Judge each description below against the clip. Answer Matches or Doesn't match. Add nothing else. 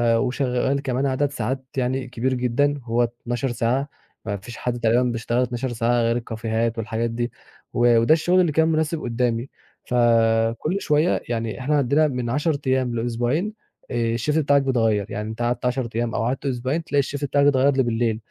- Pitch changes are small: Doesn't match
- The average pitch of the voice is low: Matches